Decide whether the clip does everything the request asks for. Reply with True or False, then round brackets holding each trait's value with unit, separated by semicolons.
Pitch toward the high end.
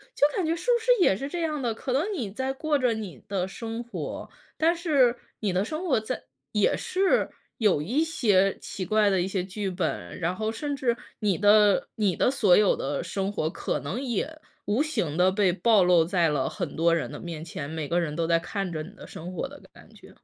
True (210 Hz)